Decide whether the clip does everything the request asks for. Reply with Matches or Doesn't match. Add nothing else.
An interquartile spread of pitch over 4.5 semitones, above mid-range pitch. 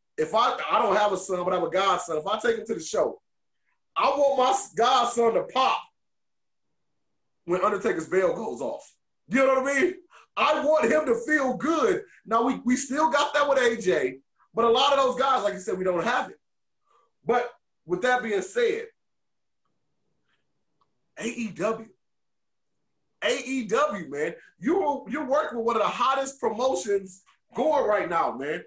Matches